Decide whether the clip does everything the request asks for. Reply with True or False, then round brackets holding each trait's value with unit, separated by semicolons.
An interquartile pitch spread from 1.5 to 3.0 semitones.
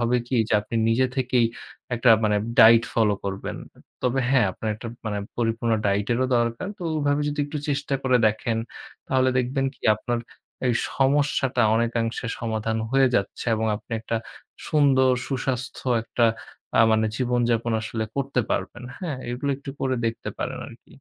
True (2.7 semitones)